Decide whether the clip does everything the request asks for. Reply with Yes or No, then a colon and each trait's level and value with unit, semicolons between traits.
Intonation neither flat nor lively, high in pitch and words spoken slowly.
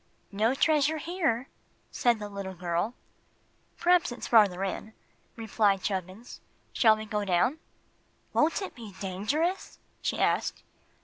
No: wide, 6.1 semitones; high, 220 Hz; slow, 125 wpm